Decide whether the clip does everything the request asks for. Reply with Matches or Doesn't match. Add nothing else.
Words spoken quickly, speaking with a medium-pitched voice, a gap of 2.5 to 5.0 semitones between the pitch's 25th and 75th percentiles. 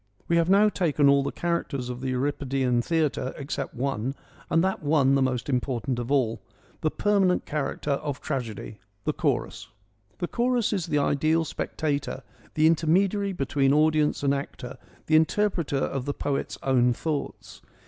Doesn't match